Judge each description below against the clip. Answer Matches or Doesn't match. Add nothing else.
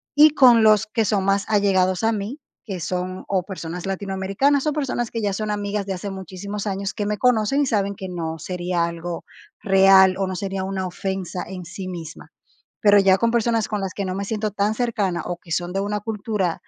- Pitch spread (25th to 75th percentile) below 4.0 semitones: Matches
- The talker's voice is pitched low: Doesn't match